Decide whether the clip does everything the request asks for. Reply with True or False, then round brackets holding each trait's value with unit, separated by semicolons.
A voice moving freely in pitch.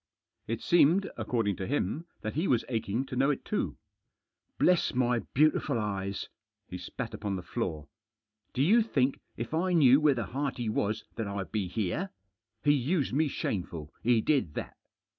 True (5.8 semitones)